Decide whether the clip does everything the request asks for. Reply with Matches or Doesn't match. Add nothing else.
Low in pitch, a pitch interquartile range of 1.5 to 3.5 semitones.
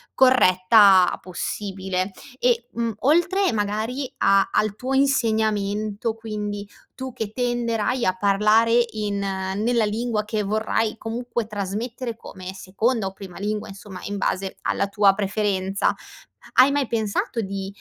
Doesn't match